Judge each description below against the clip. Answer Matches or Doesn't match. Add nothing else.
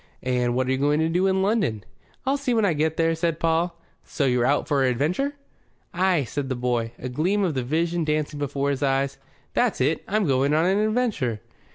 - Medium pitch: Matches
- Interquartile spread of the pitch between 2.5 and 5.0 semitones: Doesn't match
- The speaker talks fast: Matches